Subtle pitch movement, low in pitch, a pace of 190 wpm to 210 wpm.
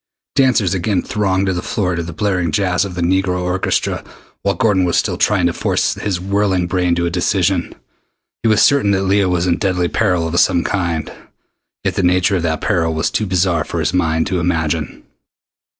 Yes: narrow, 2.3 semitones; very low, 90 Hz; average, 200 wpm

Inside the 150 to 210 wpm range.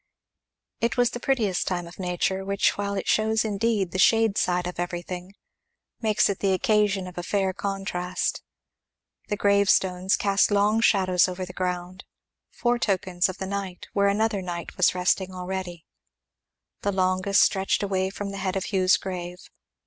Yes: average, 160 wpm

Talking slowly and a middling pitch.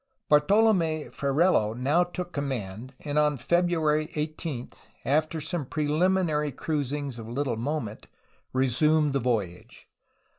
Yes: slow, 110 wpm; medium, 150 Hz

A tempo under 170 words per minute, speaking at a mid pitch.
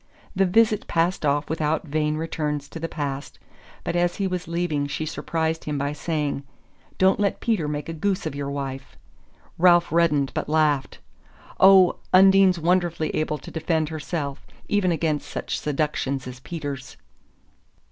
Yes: average, 155 wpm; medium, 160 Hz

